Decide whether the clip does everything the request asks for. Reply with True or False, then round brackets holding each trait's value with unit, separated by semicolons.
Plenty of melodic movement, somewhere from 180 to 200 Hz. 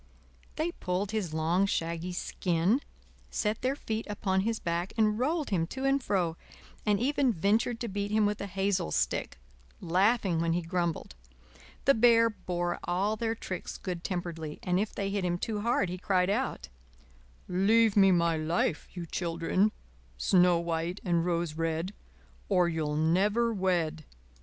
False (4.0 semitones; 185 Hz)